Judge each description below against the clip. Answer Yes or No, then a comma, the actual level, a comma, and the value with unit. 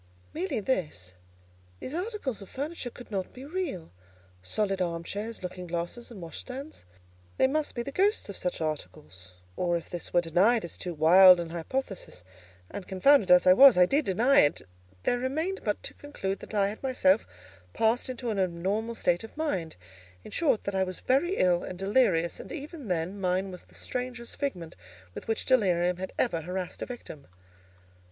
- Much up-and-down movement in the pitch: Yes, wide, 6.8 semitones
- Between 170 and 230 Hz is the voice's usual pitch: Yes, high, 190 Hz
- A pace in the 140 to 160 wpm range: No, average, 175 wpm